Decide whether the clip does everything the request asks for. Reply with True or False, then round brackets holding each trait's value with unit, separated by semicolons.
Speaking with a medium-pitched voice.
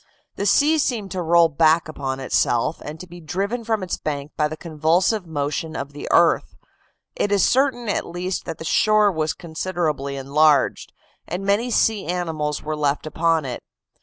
True (165 Hz)